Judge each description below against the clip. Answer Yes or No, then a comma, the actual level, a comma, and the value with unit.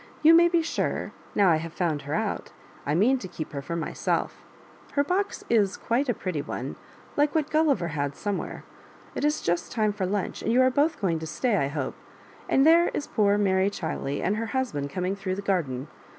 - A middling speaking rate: No, fast, 210 wpm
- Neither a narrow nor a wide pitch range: No, wide, 7.9 semitones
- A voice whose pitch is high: Yes, high, 200 Hz